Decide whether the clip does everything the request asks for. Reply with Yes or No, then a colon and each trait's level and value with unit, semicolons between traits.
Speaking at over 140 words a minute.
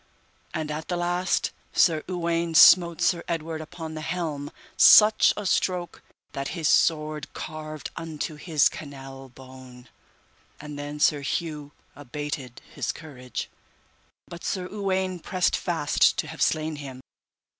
No: slow, 135 wpm